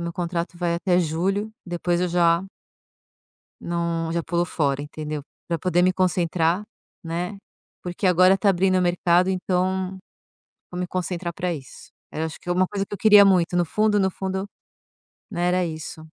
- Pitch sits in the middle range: Yes, medium, 175 Hz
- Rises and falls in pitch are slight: Yes, narrow, 1.7 semitones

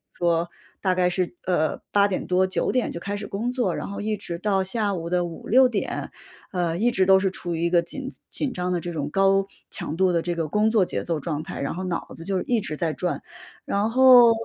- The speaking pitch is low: No, medium, 185 Hz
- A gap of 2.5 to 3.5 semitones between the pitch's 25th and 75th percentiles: Yes, average, 3.2 semitones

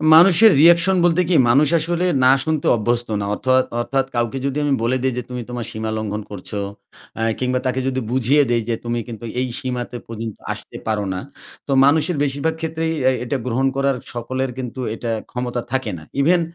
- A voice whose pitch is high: No, low, 130 Hz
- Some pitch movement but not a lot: Yes, average, 3.7 semitones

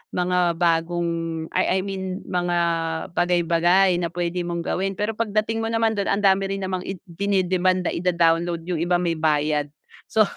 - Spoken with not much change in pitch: Yes, narrow, 2.2 semitones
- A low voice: No, medium, 180 Hz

